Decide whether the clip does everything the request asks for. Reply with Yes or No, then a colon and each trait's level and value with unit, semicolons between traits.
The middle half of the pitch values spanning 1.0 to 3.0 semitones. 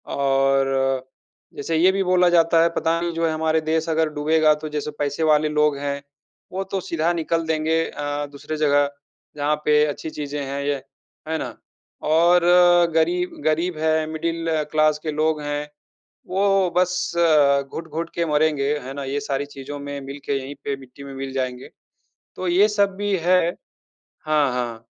Yes: average, 2.7 semitones